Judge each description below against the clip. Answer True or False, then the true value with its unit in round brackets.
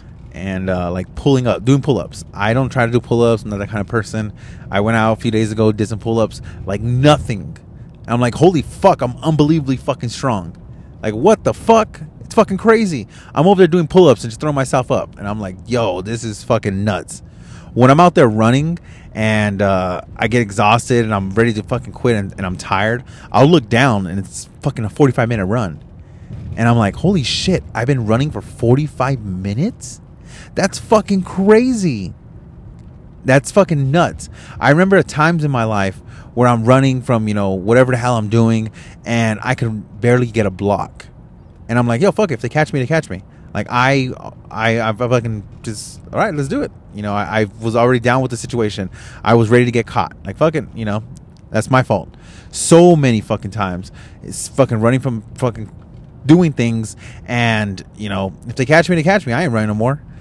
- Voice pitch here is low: True (115 Hz)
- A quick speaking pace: True (215 wpm)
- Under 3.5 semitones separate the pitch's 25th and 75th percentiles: False (4.1 semitones)